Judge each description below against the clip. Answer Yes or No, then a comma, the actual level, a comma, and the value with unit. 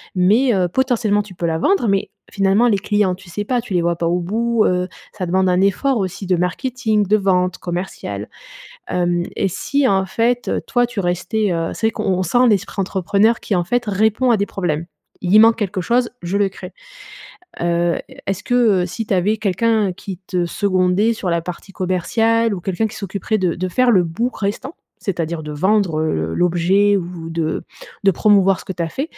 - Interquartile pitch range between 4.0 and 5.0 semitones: No, average, 3.6 semitones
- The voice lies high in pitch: Yes, high, 195 Hz